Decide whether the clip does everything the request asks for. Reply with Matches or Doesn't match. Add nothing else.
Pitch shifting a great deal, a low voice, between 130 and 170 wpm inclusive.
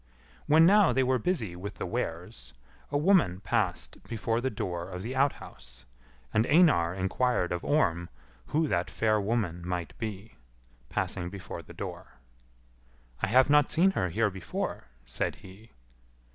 Matches